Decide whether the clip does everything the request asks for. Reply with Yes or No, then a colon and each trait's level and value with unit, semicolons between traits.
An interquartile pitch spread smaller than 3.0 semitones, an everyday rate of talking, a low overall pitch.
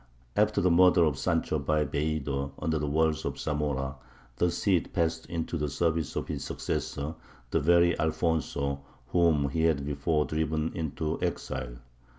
Yes: narrow, 2.6 semitones; average, 155 wpm; very low, 80 Hz